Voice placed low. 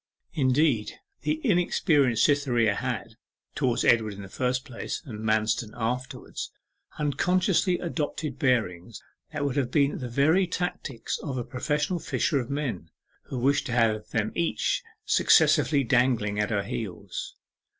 Yes: low, 130 Hz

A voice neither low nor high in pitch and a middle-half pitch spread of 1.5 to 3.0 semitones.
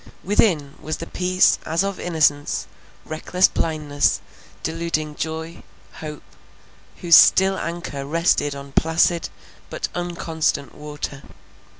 Yes: medium, 160 Hz; average, 2.7 semitones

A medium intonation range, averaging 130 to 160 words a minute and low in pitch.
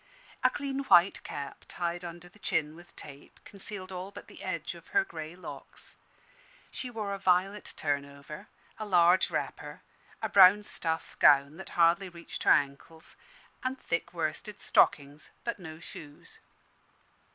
No: average, 4.1 semitones; average, 150 wpm; medium, 175 Hz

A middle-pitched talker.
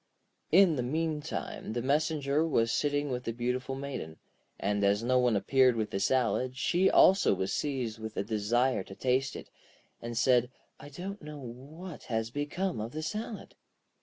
No: low, 130 Hz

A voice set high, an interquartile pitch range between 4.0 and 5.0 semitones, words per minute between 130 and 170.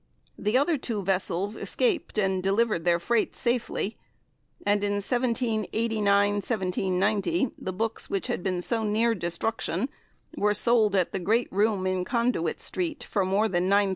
No: high, 210 Hz; average, 3.3 semitones; average, 150 wpm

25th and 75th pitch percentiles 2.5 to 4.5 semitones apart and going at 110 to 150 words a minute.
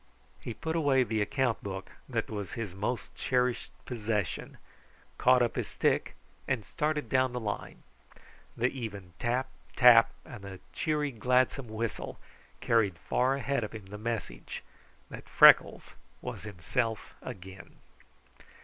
Yes: average, 3.7 semitones; slow, 135 wpm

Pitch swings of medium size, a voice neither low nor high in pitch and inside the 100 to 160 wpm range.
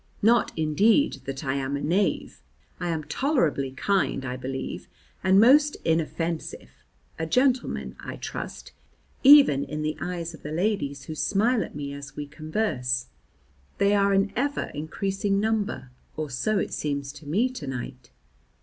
No: wide, 6.6 semitones; medium, 160 Hz; average, 155 wpm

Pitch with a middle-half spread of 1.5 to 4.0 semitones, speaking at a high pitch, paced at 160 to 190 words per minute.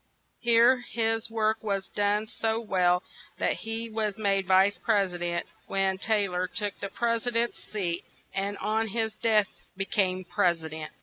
Yes: average, 2.9 semitones; high, 205 Hz; average, 180 wpm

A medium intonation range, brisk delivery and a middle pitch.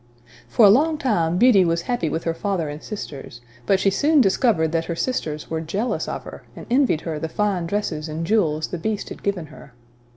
Yes: average, 4.9 semitones; fast, 215 wpm; medium, 175 Hz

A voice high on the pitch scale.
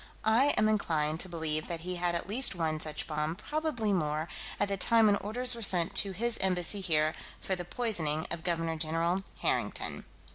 No: medium, 175 Hz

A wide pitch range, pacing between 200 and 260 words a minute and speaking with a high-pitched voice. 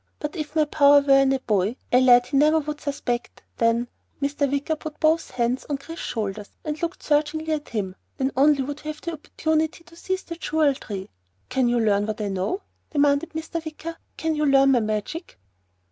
No: average, 4.3 semitones; fast, 205 wpm; very high, 285 Hz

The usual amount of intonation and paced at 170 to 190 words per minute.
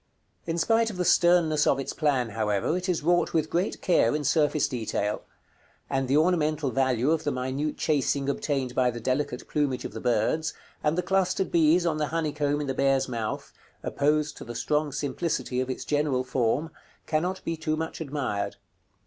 Yes: average, 3.8 semitones; average, 185 wpm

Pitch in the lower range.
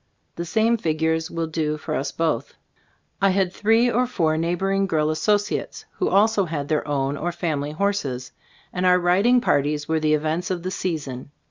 No: medium, 165 Hz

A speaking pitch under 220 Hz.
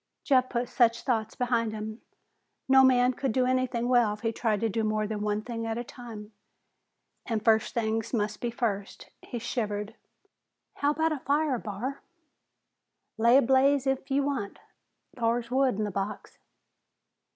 No: high, 235 Hz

